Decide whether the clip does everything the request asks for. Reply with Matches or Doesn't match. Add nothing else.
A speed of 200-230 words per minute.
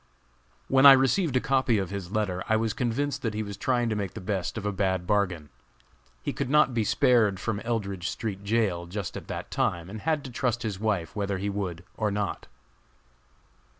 Matches